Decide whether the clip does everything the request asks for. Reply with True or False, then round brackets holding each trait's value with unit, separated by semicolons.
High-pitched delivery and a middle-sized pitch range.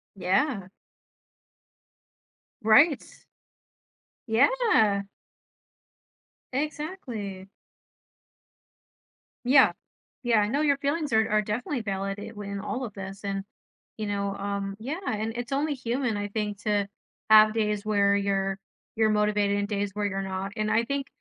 True (210 Hz; 3.6 semitones)